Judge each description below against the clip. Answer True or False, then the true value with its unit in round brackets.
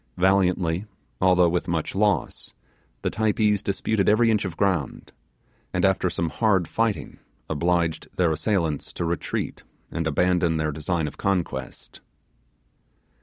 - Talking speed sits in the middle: False (125 wpm)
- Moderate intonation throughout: True (3.2 semitones)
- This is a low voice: True (90 Hz)